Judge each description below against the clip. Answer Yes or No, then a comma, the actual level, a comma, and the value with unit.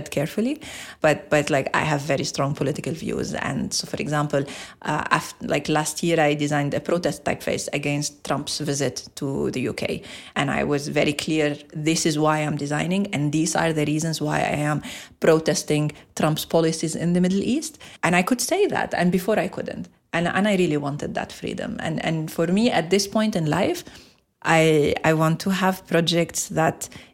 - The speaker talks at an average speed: Yes, average, 190 wpm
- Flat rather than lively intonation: No, average, 3.4 semitones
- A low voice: No, medium, 160 Hz